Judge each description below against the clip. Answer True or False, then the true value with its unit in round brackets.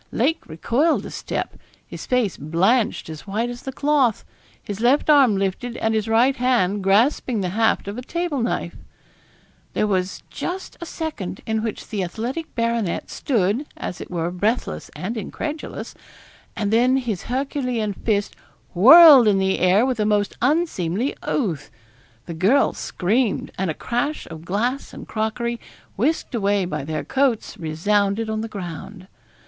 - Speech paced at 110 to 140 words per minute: False (155 wpm)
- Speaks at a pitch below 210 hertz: False (220 Hz)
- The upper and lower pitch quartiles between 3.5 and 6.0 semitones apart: True (4.8 semitones)